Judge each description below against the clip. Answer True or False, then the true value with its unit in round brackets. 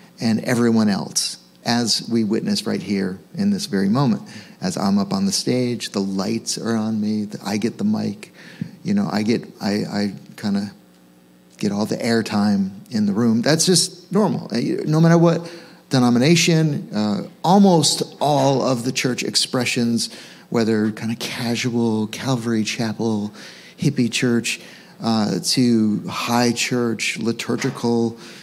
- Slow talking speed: False (145 wpm)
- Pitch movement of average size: False (8.0 semitones)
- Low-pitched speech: True (120 Hz)